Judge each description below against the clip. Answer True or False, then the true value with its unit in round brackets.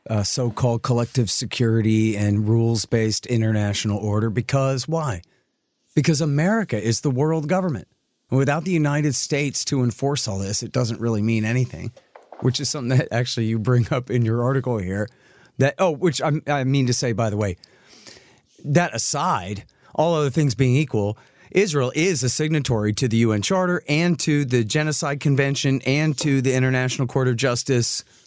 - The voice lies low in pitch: True (130 Hz)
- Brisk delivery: False (170 wpm)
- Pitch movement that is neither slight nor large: True (4.1 semitones)